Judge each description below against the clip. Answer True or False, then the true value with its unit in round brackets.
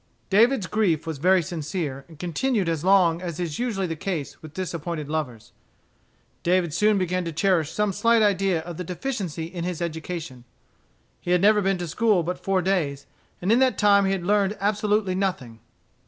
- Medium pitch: True (180 Hz)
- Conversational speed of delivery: True (185 wpm)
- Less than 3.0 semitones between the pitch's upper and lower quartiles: False (3.5 semitones)